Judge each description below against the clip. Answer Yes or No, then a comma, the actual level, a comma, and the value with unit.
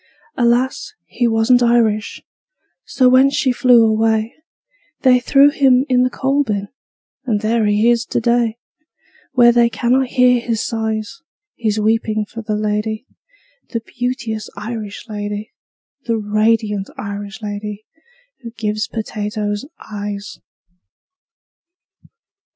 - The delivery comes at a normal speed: No, slow, 120 wpm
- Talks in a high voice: Yes, high, 225 Hz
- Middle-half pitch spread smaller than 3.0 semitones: Yes, narrow, 2.5 semitones